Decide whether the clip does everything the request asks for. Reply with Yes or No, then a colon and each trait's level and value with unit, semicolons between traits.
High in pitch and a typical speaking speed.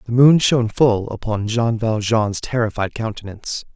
No: low, 115 Hz; average, 145 wpm